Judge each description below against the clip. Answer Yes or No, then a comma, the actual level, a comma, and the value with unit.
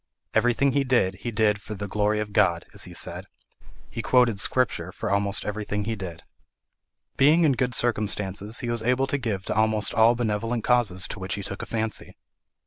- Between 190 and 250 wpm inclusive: Yes, average, 195 wpm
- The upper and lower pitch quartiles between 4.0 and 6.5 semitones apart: No, average, 3.1 semitones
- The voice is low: Yes, low, 110 Hz